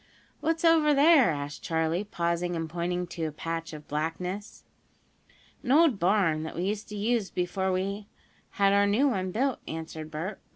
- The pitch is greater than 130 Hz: Yes, medium, 185 Hz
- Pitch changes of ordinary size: Yes, average, 4.4 semitones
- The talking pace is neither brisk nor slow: Yes, average, 170 wpm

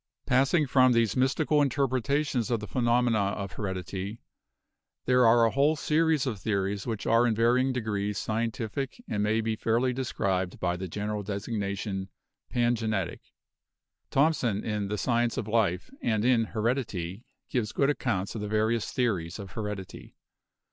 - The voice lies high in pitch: No, low, 115 Hz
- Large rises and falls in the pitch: No, average, 3.7 semitones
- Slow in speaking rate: No, average, 155 wpm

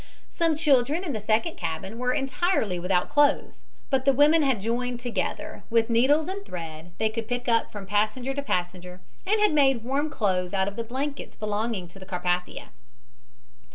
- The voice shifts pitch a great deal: Yes, wide, 6.4 semitones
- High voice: Yes, high, 235 Hz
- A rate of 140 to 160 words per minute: No, average, 180 wpm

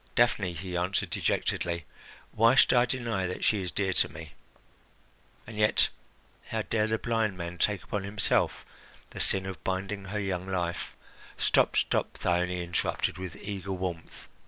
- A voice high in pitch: No, very low, 95 Hz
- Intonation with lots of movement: No, average, 3.0 semitones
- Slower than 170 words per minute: Yes, average, 160 wpm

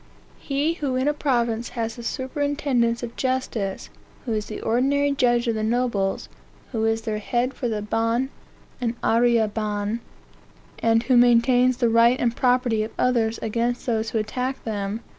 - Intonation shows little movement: Yes, narrow, 2.3 semitones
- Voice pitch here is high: Yes, high, 235 Hz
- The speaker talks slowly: No, average, 165 wpm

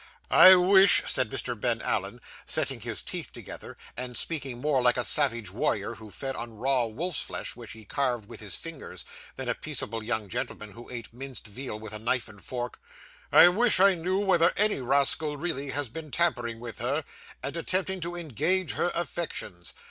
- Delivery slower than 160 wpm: No, average, 185 wpm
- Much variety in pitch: Yes, wide, 6.2 semitones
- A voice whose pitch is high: No, low, 130 Hz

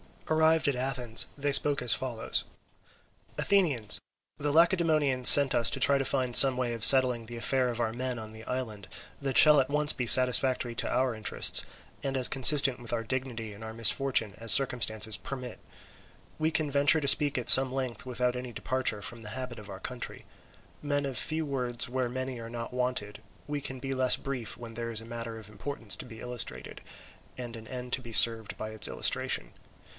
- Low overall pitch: Yes, low, 125 Hz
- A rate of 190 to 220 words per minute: Yes, average, 200 wpm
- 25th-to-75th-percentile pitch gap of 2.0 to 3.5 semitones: Yes, average, 2.8 semitones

